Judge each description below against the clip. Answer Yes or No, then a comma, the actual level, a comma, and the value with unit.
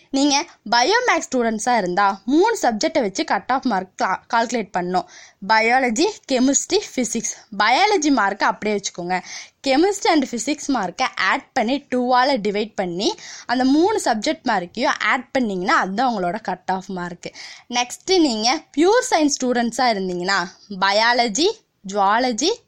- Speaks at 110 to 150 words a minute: Yes, average, 125 wpm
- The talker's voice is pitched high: Yes, very high, 250 Hz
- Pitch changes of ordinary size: No, wide, 6.6 semitones